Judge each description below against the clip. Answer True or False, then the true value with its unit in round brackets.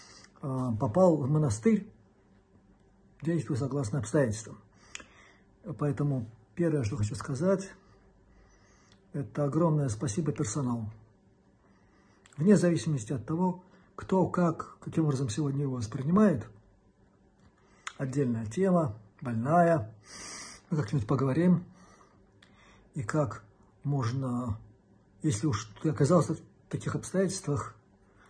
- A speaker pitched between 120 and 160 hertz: True (140 Hz)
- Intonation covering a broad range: True (7.1 semitones)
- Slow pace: True (90 wpm)